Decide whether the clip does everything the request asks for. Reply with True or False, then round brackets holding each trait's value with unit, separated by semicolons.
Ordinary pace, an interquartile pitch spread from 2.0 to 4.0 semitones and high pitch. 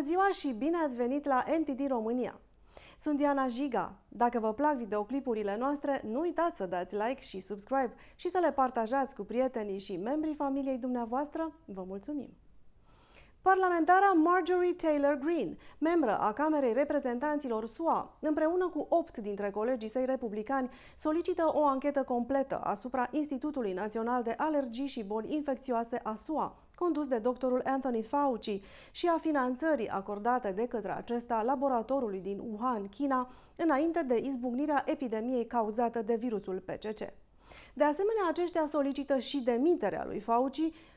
False (145 wpm; 4.4 semitones; 265 Hz)